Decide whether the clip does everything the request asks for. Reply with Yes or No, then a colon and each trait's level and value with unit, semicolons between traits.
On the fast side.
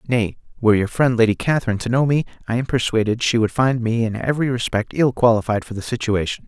Yes: fast, 220 wpm